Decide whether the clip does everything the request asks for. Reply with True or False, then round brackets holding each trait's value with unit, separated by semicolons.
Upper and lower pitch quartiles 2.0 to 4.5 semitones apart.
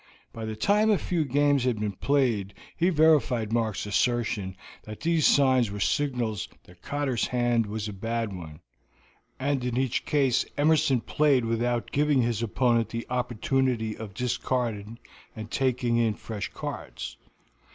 True (3.7 semitones)